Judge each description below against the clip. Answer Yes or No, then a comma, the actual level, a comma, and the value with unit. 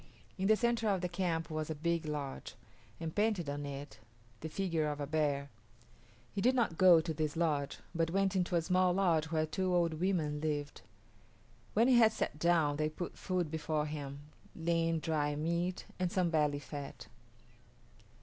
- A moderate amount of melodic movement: Yes, average, 3.4 semitones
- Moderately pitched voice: Yes, medium, 165 Hz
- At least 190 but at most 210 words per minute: No, average, 180 wpm